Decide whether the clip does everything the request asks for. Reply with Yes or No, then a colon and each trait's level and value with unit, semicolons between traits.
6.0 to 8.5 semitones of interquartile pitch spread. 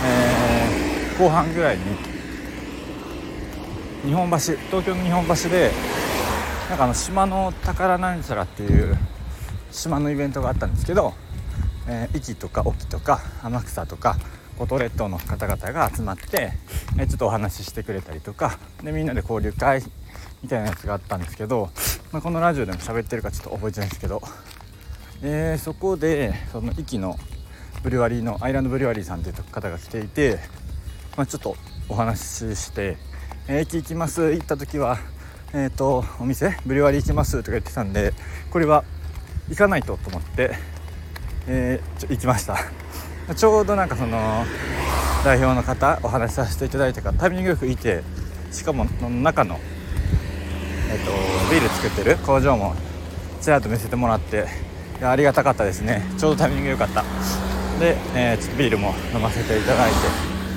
Yes: wide, 7.5 semitones